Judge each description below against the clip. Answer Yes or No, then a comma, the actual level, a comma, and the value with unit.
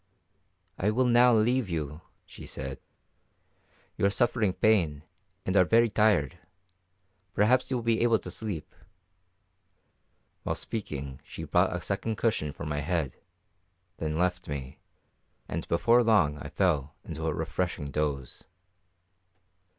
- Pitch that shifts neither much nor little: No, wide, 7.0 semitones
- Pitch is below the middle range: Yes, very low, 90 Hz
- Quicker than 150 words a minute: No, slow, 135 wpm